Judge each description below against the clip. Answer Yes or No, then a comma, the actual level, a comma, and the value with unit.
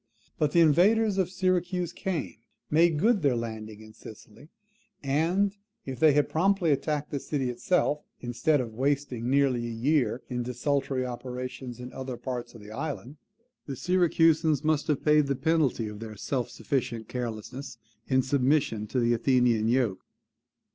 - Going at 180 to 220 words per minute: No, average, 155 wpm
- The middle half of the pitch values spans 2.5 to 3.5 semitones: No, average, 4.5 semitones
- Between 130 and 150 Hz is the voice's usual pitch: Yes, low, 135 Hz